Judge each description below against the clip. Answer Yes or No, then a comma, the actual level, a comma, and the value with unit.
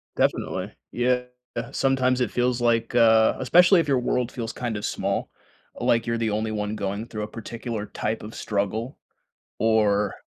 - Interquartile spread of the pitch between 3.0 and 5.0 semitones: No, narrow, 2.5 semitones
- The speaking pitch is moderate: No, low, 115 Hz